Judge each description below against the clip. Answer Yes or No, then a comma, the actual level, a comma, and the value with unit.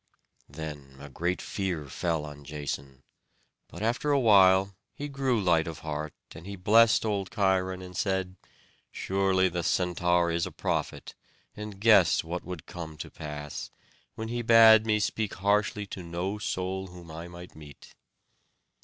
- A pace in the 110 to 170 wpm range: Yes, average, 155 wpm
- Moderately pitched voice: No, very low, 90 Hz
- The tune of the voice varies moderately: Yes, average, 4.2 semitones